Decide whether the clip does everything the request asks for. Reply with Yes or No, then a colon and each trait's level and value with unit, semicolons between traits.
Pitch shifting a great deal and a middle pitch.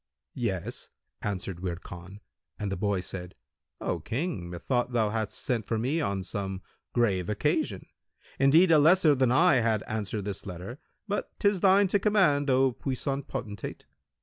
No: wide, 6.7 semitones; low, 115 Hz